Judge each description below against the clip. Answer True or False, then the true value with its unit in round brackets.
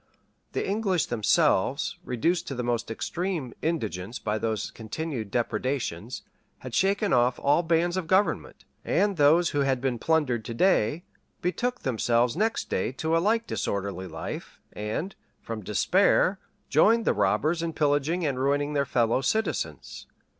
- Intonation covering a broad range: True (7.0 semitones)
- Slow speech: False (145 wpm)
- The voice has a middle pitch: True (145 Hz)